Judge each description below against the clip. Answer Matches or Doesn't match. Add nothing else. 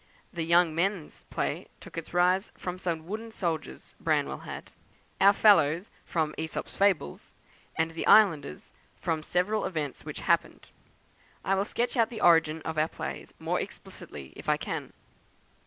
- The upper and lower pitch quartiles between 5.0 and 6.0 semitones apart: Doesn't match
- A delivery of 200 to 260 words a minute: Doesn't match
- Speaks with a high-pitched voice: Doesn't match